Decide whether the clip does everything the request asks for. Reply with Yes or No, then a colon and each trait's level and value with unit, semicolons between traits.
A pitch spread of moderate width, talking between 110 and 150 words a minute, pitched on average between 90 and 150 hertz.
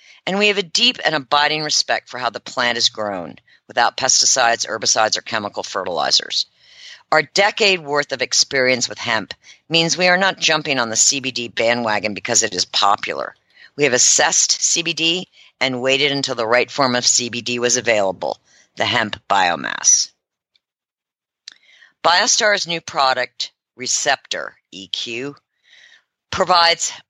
No: wide, 5.8 semitones; average, 140 wpm; medium, 140 Hz